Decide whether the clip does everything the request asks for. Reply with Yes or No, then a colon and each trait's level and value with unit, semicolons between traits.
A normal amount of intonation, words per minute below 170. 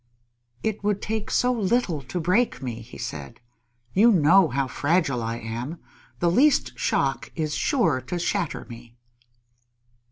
No: wide, 8.5 semitones; average, 140 wpm